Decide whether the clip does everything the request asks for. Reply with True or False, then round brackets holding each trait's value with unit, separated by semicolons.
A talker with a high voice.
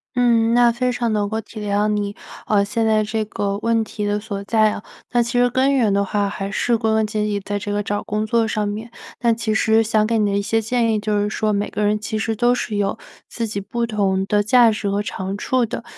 True (215 Hz)